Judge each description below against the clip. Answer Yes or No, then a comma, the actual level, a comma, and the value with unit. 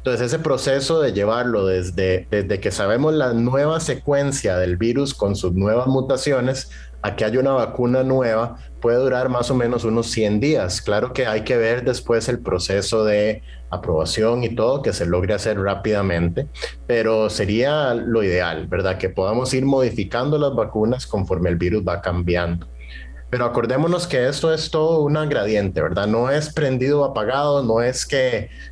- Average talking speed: Yes, average, 170 wpm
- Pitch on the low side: Yes, low, 115 Hz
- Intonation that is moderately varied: No, wide, 5.7 semitones